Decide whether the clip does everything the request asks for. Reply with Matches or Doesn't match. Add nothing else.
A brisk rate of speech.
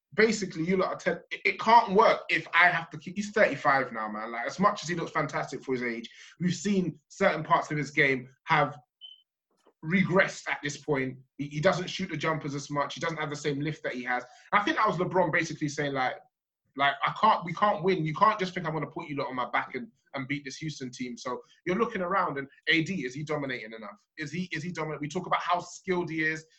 Matches